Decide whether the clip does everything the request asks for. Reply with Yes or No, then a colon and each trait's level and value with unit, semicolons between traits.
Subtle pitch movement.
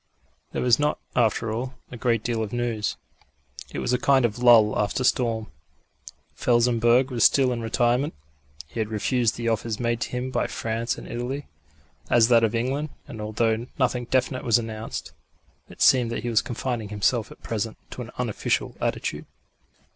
Yes: narrow, 1.8 semitones